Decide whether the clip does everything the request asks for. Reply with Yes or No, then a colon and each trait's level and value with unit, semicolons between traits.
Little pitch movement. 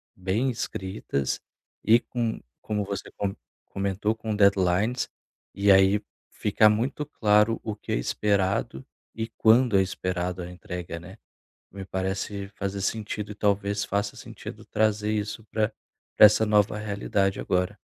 Yes: narrow, 2.0 semitones